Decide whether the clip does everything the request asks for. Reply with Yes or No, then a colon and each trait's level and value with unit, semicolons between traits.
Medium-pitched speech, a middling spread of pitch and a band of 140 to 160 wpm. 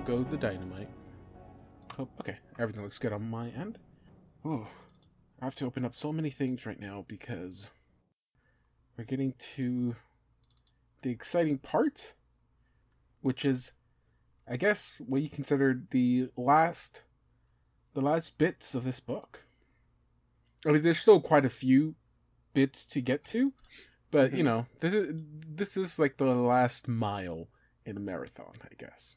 No: low, 130 Hz; average, 4.3 semitones; average, 145 wpm